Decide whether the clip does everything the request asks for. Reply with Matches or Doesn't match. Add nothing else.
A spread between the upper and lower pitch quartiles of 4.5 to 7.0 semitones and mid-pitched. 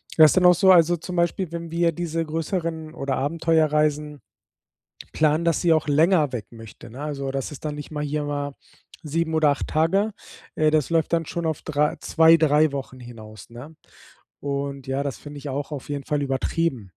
Doesn't match